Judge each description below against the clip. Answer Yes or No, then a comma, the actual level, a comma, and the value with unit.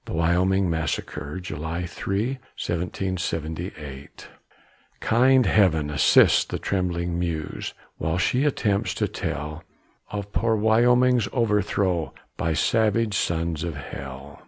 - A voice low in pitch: Yes, very low, 90 Hz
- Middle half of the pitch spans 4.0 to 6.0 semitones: Yes, average, 4.6 semitones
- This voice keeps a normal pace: No, slow, 110 wpm